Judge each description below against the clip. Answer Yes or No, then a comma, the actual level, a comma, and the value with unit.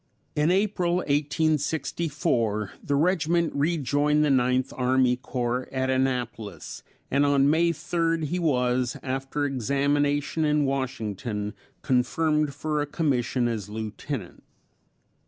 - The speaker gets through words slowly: Yes, slow, 110 wpm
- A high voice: No, medium, 140 Hz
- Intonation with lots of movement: No, average, 3.5 semitones